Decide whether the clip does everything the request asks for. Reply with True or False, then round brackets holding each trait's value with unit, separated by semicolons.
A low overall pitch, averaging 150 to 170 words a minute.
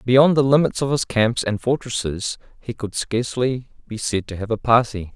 False (120 Hz; 200 wpm)